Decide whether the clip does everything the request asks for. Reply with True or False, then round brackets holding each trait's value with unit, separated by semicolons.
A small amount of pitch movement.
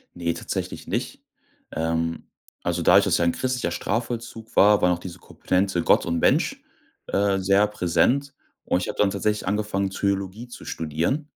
False (3.7 semitones)